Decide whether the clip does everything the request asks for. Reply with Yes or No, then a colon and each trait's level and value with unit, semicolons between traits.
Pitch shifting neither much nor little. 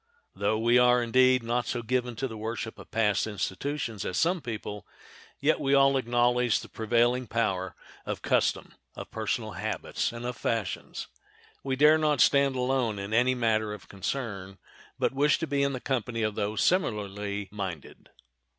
Yes: average, 3.4 semitones